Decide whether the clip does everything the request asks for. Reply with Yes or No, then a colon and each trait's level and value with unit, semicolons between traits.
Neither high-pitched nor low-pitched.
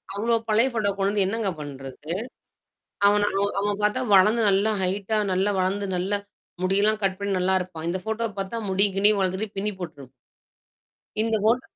No: high, 200 Hz